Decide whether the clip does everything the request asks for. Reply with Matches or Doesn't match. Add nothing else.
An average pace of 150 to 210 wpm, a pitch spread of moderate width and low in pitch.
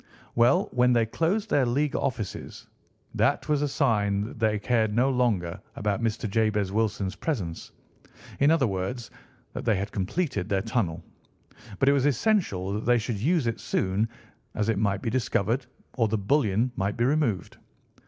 Matches